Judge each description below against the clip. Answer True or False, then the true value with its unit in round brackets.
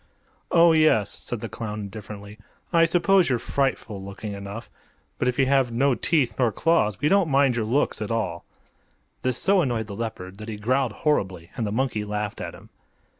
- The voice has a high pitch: False (115 Hz)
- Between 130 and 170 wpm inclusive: False (190 wpm)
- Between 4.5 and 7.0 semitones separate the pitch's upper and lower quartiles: True (5.0 semitones)